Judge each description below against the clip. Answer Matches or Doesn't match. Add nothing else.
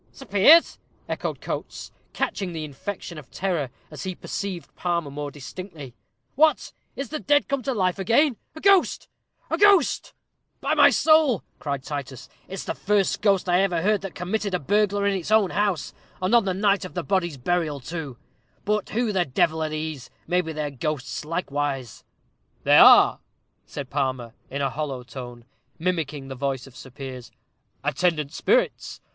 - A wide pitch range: Matches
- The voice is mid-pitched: Matches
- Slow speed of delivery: Doesn't match